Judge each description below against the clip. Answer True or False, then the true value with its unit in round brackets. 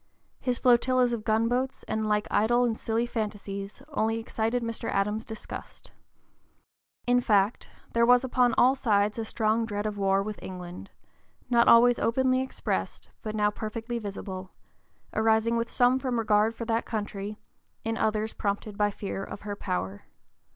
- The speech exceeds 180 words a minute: False (160 wpm)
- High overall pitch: True (220 Hz)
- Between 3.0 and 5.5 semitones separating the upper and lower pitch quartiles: False (2.4 semitones)